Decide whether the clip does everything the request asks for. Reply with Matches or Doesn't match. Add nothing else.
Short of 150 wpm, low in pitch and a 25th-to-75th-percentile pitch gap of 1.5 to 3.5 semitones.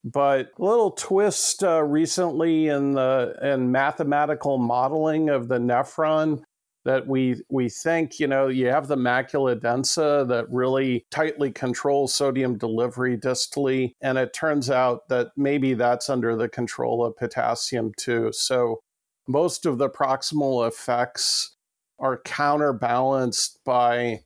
Matches